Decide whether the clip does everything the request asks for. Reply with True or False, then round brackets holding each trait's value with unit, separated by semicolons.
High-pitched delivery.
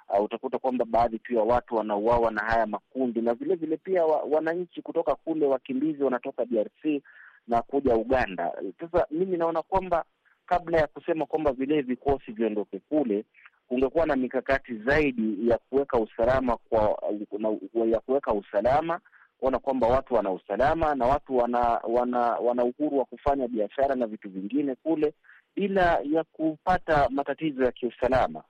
False (135 Hz)